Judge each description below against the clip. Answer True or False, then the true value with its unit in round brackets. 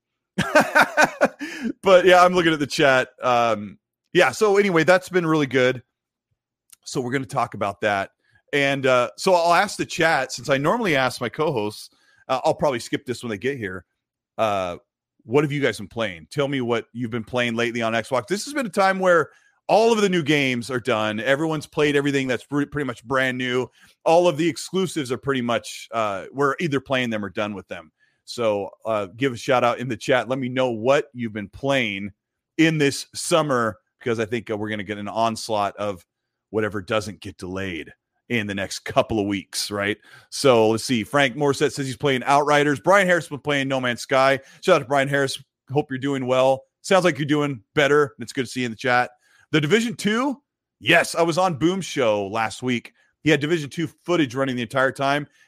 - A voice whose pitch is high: False (135 Hz)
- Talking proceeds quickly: True (215 wpm)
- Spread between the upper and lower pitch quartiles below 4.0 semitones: False (4.9 semitones)